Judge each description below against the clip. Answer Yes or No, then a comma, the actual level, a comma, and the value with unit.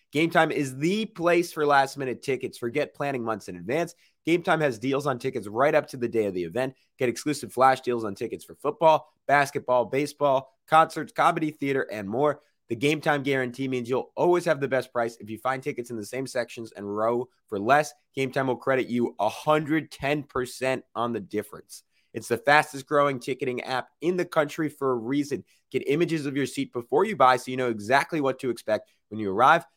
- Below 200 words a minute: No, fast, 205 wpm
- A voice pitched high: No, low, 135 Hz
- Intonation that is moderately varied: Yes, average, 3.5 semitones